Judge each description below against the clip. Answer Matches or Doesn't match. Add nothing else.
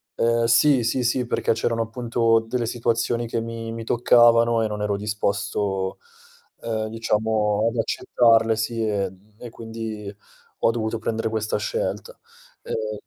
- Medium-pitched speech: Doesn't match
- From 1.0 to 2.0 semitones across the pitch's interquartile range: Matches